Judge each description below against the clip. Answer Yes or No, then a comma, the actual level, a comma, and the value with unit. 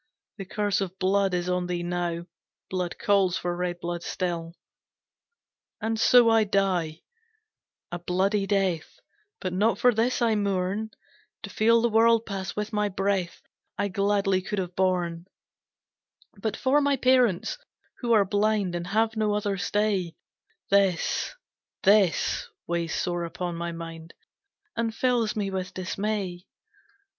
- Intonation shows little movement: No, average, 3.3 semitones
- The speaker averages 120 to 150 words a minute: Yes, average, 140 wpm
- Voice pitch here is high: Yes, high, 195 Hz